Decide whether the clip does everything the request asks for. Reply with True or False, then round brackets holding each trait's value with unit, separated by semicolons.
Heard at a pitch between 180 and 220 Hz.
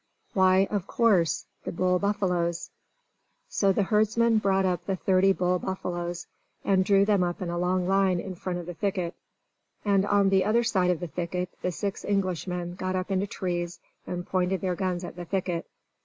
True (185 Hz)